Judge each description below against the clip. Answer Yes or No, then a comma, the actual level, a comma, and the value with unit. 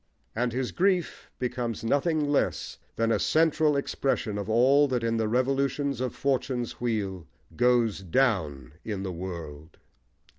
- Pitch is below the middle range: Yes, low, 120 Hz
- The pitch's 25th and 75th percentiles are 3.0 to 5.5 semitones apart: Yes, average, 5.0 semitones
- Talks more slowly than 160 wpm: Yes, average, 140 wpm